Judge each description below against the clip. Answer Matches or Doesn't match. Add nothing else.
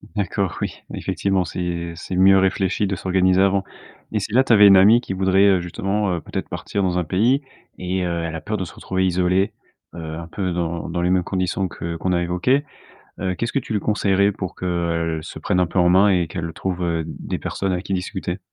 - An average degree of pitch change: Doesn't match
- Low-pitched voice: Matches